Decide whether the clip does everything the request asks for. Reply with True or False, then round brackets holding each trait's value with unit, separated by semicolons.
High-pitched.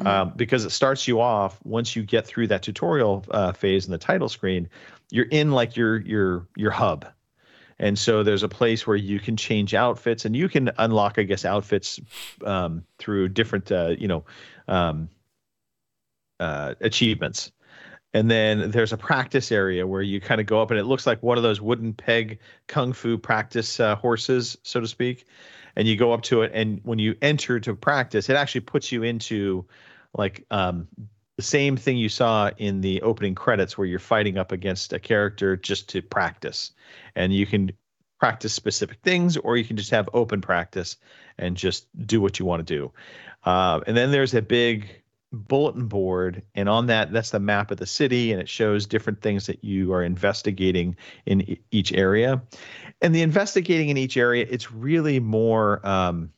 False (110 Hz)